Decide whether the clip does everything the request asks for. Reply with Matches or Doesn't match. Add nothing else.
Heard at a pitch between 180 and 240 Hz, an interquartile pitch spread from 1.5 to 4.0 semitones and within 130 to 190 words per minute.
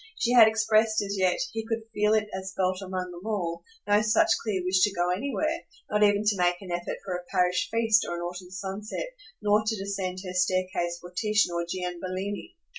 Doesn't match